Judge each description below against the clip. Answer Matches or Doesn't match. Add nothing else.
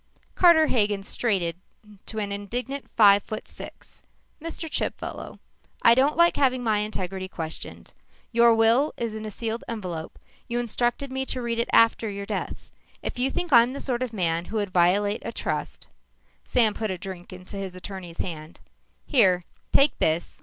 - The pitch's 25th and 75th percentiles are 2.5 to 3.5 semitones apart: Doesn't match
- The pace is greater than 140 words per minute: Matches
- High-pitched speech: Matches